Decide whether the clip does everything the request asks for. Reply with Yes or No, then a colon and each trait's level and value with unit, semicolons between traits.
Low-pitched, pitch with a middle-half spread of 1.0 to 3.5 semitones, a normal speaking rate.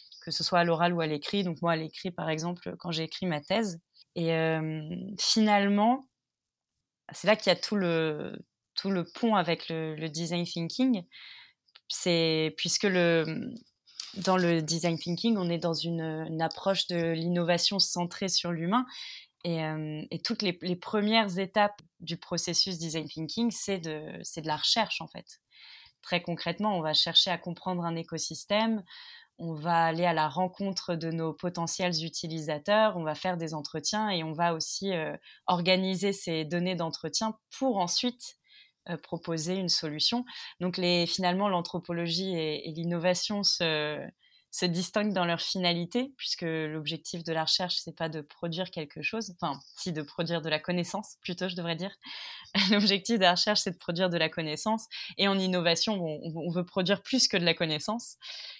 No: medium, 175 Hz; average, 3.0 semitones; average, 175 wpm